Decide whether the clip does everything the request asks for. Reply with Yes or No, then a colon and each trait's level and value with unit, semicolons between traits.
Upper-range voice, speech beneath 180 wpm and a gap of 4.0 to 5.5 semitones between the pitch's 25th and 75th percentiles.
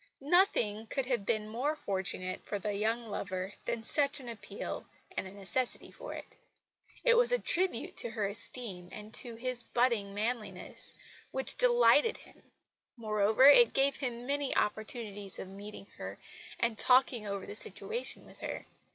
Yes: high, 230 Hz; average, 160 wpm; average, 4.7 semitones